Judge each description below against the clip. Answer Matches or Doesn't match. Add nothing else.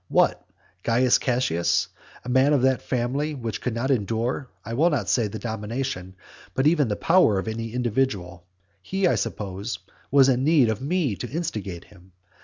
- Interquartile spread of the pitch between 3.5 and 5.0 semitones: Matches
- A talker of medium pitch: Doesn't match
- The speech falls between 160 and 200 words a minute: Matches